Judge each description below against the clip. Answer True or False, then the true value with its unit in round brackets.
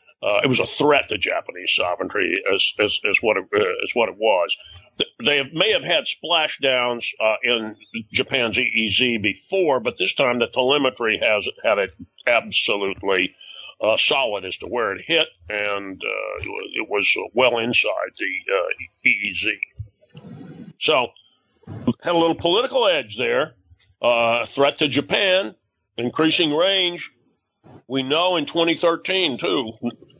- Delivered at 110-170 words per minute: True (145 wpm)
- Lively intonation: True (8.4 semitones)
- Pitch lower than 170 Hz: True (140 Hz)